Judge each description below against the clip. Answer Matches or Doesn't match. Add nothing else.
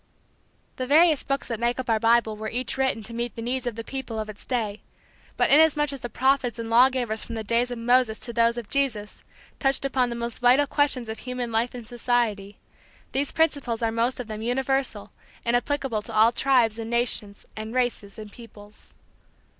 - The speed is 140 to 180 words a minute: Doesn't match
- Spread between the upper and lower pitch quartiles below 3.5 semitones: Matches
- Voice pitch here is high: Matches